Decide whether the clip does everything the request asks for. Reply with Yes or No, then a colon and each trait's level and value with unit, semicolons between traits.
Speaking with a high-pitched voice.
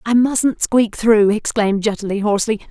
Yes: high, 215 Hz